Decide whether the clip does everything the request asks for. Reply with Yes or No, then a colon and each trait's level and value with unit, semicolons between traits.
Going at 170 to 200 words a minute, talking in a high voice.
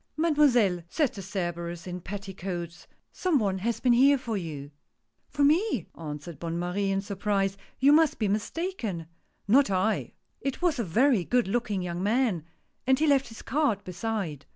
Yes: average, 190 wpm; high, 205 Hz